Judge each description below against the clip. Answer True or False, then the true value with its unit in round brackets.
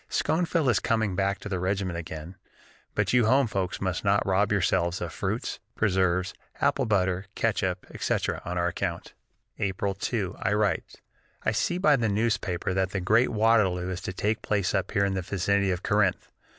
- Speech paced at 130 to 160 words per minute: False (185 wpm)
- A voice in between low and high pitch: False (100 Hz)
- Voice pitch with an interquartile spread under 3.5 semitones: True (2.6 semitones)